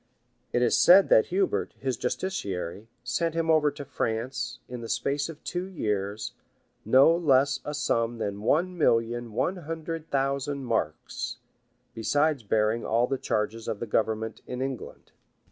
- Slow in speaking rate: No, average, 155 wpm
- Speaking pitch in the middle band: No, low, 130 Hz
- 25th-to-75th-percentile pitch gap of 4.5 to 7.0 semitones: Yes, average, 5.1 semitones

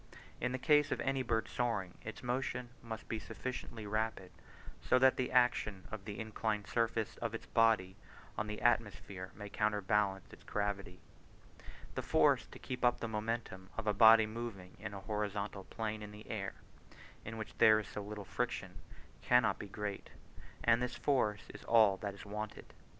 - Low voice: Yes, low, 110 Hz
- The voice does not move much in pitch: Yes, narrow, 2.3 semitones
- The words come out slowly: No, average, 175 wpm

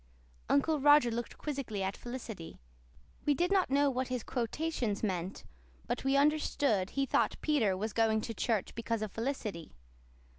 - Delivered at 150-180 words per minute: Yes, average, 160 wpm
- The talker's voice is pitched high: Yes, high, 240 Hz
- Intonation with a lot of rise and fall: No, average, 4.8 semitones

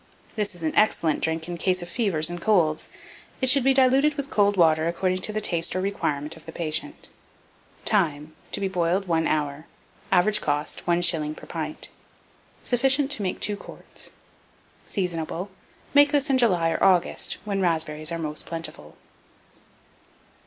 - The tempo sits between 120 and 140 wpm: No, average, 160 wpm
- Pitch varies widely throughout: No, average, 4.7 semitones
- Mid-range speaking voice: Yes, medium, 175 Hz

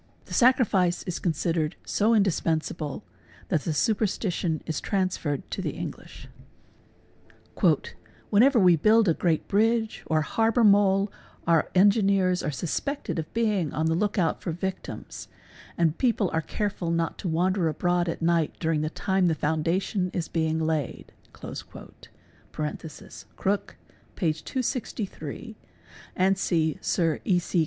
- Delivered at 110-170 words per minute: Yes, slow, 135 wpm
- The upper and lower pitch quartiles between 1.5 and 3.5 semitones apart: No, average, 3.9 semitones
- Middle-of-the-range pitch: Yes, medium, 180 Hz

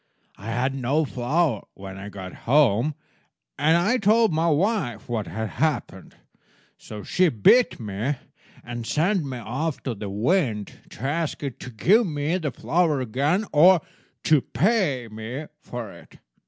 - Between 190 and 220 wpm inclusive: No, average, 155 wpm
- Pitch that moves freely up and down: Yes, wide, 6.5 semitones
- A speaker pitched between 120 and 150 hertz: Yes, medium, 140 Hz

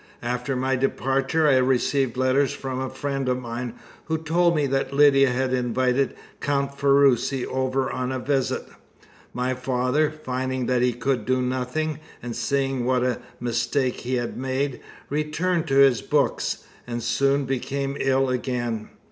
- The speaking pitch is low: Yes, low, 130 Hz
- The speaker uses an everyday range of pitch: No, narrow, 1.7 semitones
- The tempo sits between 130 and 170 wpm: Yes, average, 155 wpm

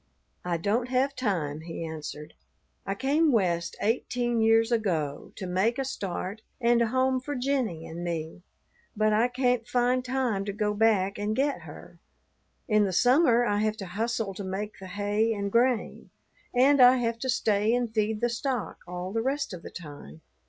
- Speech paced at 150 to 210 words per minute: Yes, average, 180 wpm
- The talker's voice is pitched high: Yes, high, 220 Hz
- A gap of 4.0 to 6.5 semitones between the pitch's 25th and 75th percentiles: Yes, average, 4.5 semitones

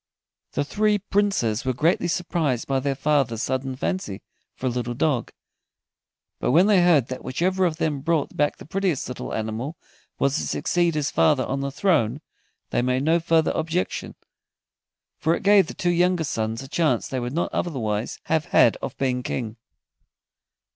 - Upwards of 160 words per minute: Yes, average, 175 wpm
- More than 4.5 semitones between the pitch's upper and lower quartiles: Yes, average, 5.2 semitones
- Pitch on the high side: No, medium, 145 Hz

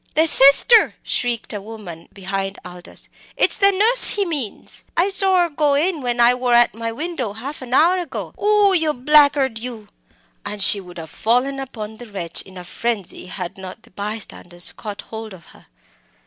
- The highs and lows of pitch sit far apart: Yes, wide, 7.0 semitones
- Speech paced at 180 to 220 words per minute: Yes, average, 185 wpm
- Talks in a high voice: Yes, high, 240 Hz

